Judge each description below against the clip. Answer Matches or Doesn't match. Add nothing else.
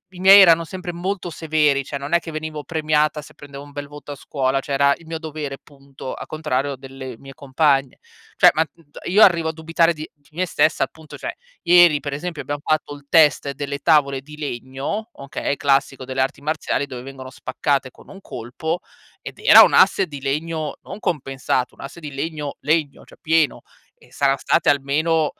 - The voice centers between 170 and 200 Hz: Doesn't match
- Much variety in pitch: Doesn't match